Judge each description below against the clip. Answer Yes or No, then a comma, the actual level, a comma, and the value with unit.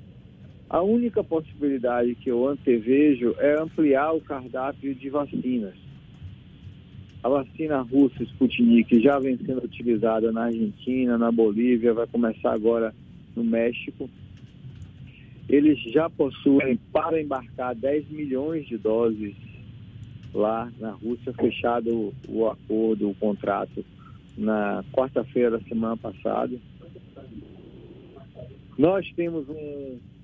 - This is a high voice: No, low, 120 Hz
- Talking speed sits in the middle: No, slow, 105 wpm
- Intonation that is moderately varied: Yes, average, 3.6 semitones